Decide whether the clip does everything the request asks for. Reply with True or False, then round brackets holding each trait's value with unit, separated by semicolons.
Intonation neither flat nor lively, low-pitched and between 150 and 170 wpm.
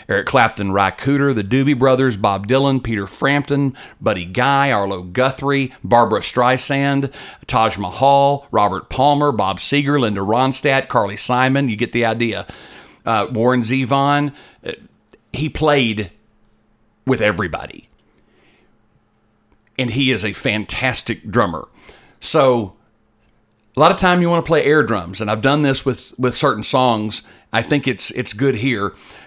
False (4.0 semitones; 125 Hz; 140 wpm)